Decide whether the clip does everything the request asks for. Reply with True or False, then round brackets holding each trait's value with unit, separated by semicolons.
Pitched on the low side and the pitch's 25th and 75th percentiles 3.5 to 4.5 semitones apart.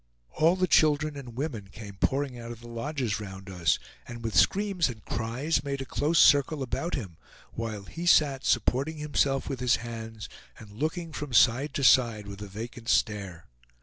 False (120 Hz; 5.0 semitones)